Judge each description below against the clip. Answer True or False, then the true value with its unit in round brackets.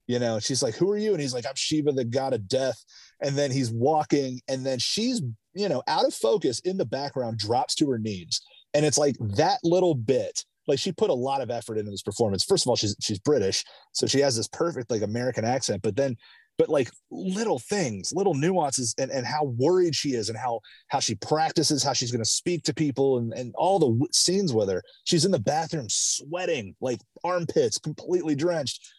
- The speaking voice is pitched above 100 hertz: True (140 Hz)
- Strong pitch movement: True (6.1 semitones)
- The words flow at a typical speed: False (225 wpm)